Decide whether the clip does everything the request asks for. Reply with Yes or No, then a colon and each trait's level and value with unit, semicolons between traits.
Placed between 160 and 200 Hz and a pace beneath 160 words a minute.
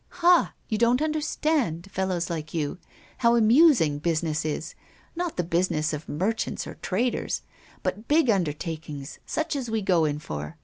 Yes: medium, 185 Hz; average, 150 wpm